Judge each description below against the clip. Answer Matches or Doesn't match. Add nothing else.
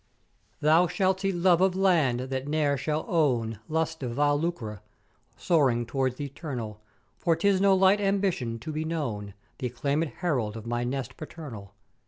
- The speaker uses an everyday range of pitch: Doesn't match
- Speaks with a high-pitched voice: Doesn't match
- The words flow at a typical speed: Matches